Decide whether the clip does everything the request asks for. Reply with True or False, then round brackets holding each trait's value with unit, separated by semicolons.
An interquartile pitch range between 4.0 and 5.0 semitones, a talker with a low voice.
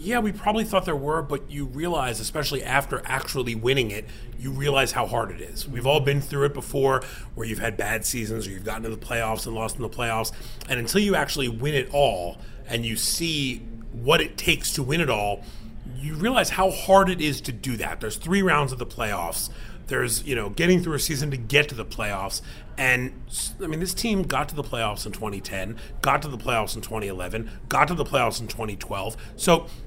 True (4.5 semitones; 125 Hz)